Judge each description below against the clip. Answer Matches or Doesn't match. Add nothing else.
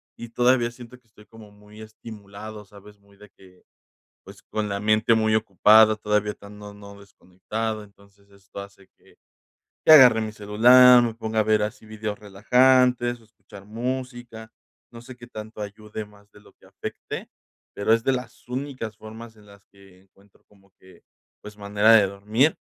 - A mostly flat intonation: Matches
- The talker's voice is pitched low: Matches